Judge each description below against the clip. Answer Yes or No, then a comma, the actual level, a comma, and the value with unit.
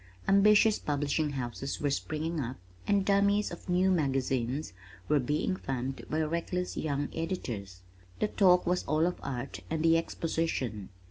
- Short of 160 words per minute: Yes, average, 145 wpm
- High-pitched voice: No, medium, 155 Hz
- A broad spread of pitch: No, average, 5.0 semitones